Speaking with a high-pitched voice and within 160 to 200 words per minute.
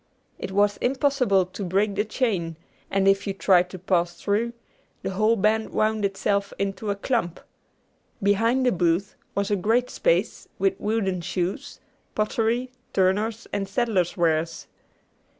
No: high, 200 Hz; average, 145 wpm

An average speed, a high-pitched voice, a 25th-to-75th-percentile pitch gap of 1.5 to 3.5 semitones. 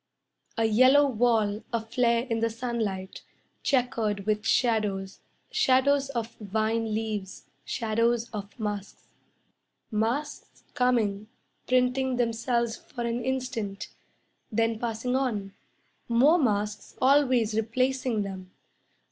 No: slow, 100 wpm; high, 230 Hz; average, 2.9 semitones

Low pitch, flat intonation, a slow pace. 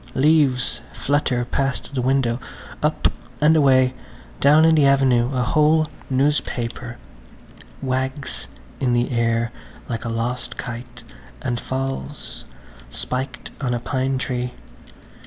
Yes: low, 130 Hz; narrow, 2.2 semitones; slow, 120 wpm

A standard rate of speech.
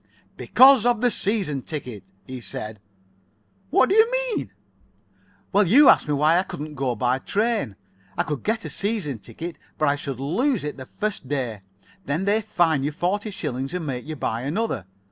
Yes: average, 185 wpm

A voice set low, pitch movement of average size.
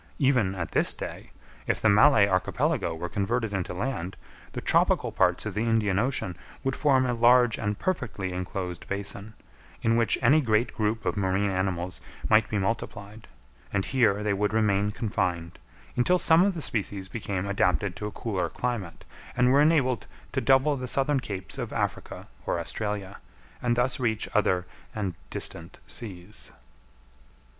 Yes: low, 105 Hz; average, 4.3 semitones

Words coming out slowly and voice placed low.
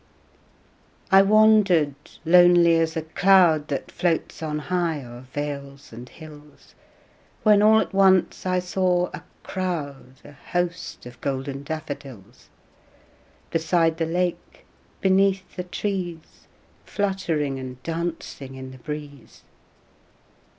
No: slow, 115 wpm; medium, 165 Hz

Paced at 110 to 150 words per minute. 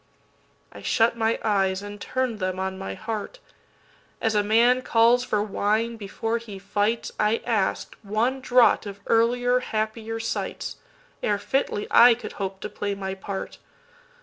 Yes: average, 140 wpm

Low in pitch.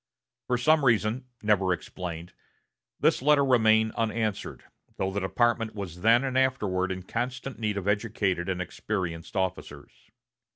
Yes: low, 105 Hz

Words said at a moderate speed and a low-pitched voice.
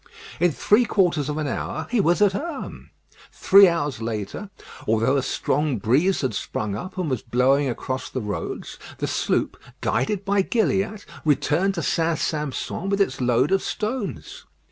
No: average, 165 wpm; medium, 155 Hz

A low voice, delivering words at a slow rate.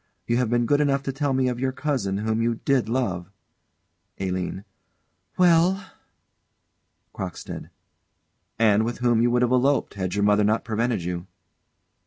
No: low, 120 Hz; average, 155 wpm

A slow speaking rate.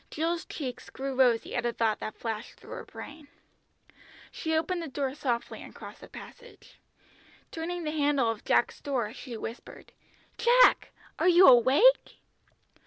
No: average, 155 wpm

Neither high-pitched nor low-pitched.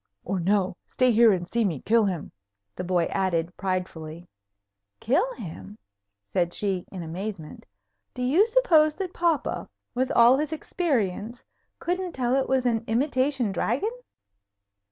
No: high, 225 Hz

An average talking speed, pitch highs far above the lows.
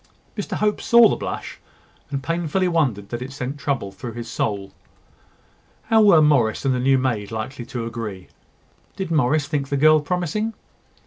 Yes: average, 170 wpm; wide, 6.0 semitones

